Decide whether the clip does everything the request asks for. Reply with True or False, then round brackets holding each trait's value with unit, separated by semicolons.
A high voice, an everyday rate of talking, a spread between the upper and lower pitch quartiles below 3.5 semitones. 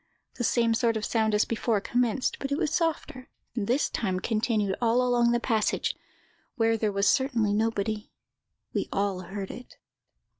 True (225 Hz; 165 wpm; 2.8 semitones)